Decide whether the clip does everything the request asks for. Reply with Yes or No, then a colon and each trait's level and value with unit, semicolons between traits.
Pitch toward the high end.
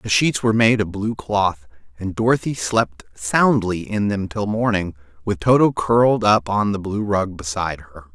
No: low, 100 Hz